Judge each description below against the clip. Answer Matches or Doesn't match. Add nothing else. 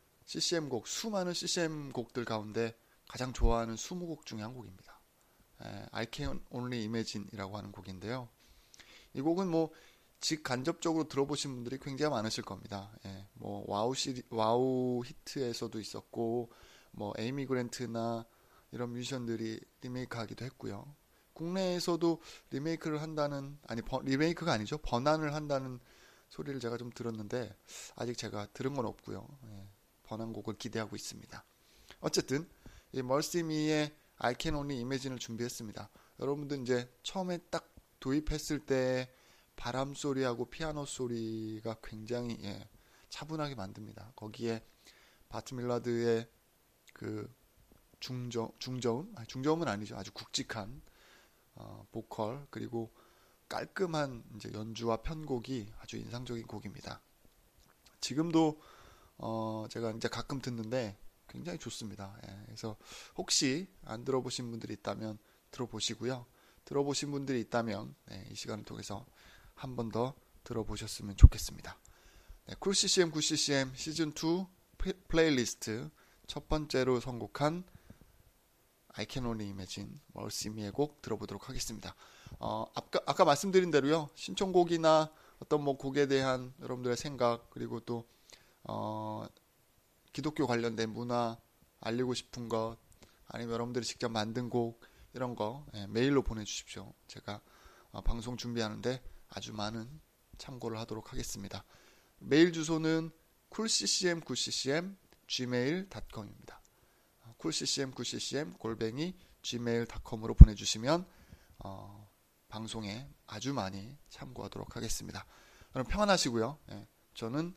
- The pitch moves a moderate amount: Matches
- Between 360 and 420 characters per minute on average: Doesn't match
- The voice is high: Doesn't match